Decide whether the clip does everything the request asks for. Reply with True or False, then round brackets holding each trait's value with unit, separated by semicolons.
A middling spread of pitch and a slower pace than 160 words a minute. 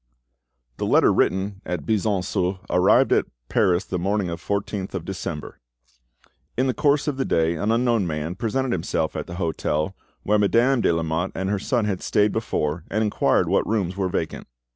False (3.9 semitones; 185 wpm)